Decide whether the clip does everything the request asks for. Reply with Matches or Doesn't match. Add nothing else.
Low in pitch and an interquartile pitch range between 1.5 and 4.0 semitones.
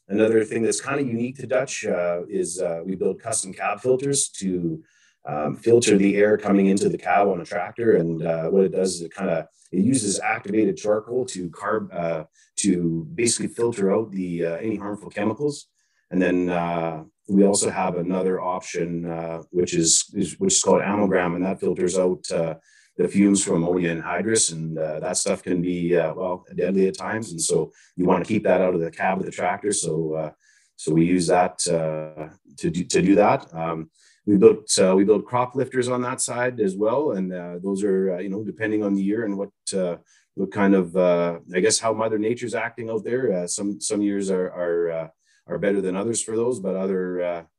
Matches